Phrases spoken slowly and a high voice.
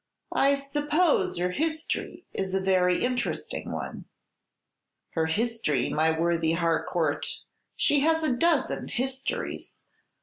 Yes: slow, 110 wpm; high, 230 Hz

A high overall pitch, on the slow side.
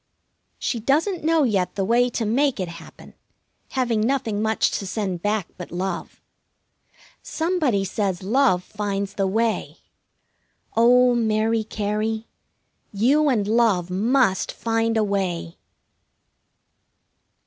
Yes: high, 220 Hz; slow, 115 wpm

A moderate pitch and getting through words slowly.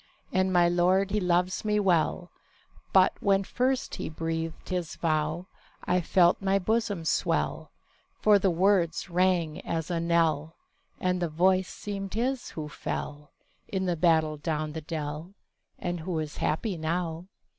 No: medium, 175 Hz; average, 150 wpm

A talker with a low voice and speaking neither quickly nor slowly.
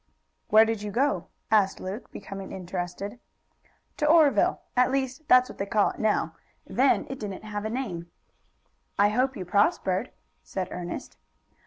No: high, 210 Hz; average, 155 wpm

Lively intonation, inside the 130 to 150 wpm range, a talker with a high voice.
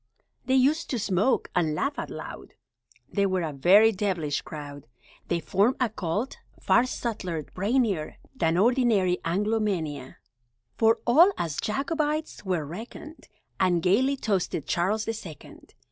Yes: wide, 6.1 semitones; average, 145 wpm; high, 200 Hz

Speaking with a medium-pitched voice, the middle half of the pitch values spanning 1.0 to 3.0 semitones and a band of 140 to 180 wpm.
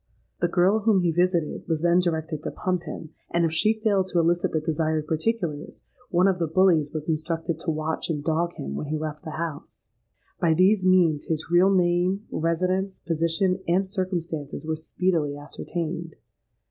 Yes: medium, 170 Hz; narrow, 2.6 semitones; average, 175 wpm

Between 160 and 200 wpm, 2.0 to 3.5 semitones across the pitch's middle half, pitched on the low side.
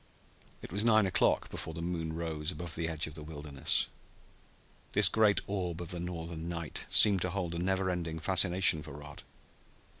Yes: average, 180 wpm; narrow, 2.6 semitones; very low, 85 Hz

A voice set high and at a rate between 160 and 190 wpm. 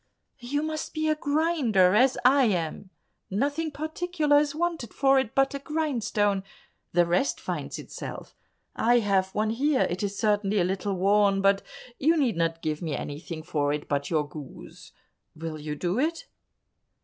Yes: high, 210 Hz; average, 165 wpm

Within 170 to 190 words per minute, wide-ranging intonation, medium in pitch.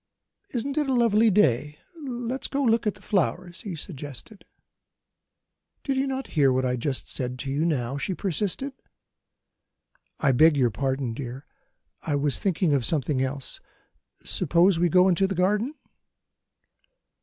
No: average, 155 wpm; wide, 7.8 semitones; medium, 170 Hz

